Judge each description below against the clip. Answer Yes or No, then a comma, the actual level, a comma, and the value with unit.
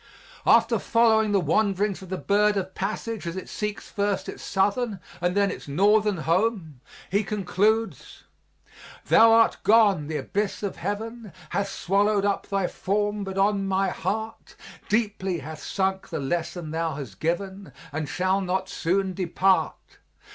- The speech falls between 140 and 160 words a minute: Yes, average, 150 wpm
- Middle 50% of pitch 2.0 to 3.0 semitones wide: Yes, average, 2.7 semitones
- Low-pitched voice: No, high, 195 Hz